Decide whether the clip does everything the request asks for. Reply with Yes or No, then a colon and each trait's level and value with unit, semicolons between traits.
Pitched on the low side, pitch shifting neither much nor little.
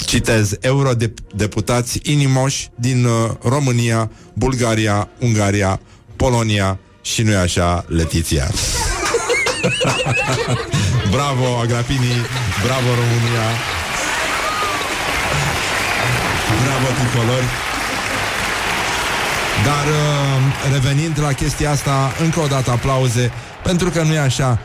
Yes: low, 120 Hz; average, 3.7 semitones